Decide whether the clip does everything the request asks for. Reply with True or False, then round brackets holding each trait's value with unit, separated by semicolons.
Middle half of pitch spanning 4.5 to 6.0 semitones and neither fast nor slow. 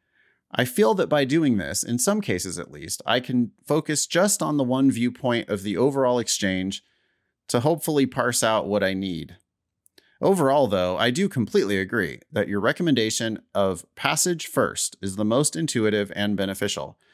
True (5.2 semitones; 170 wpm)